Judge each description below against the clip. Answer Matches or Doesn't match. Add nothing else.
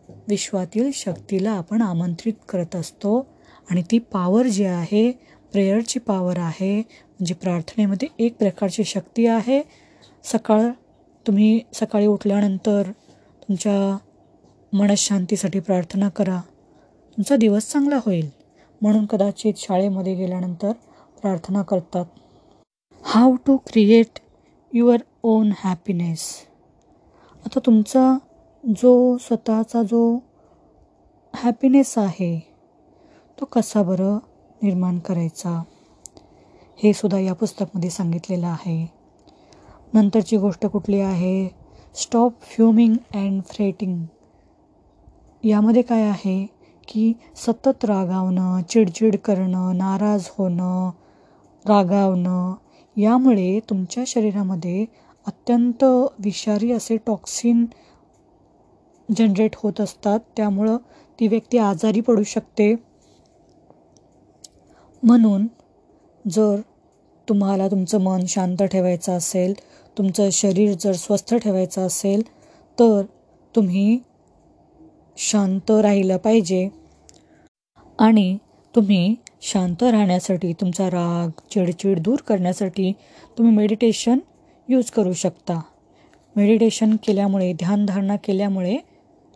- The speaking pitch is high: Matches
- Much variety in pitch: Doesn't match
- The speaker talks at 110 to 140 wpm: Doesn't match